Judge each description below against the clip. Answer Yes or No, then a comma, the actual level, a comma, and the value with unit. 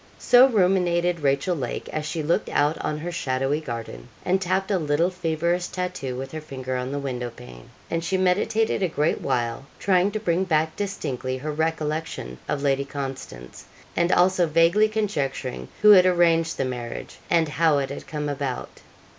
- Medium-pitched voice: Yes, medium, 160 Hz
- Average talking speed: Yes, average, 175 wpm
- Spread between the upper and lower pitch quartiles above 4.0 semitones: Yes, average, 4.8 semitones